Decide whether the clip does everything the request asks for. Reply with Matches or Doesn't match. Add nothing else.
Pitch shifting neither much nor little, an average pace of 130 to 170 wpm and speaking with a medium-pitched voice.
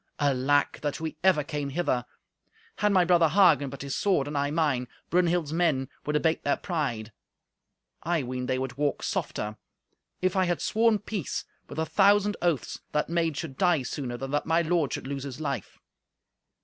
Doesn't match